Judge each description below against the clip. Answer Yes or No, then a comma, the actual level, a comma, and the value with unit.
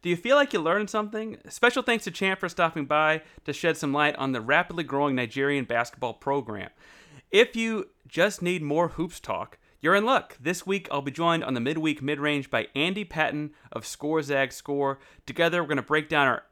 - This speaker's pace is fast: Yes, fast, 210 wpm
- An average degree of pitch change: Yes, average, 4.1 semitones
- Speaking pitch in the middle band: Yes, medium, 155 Hz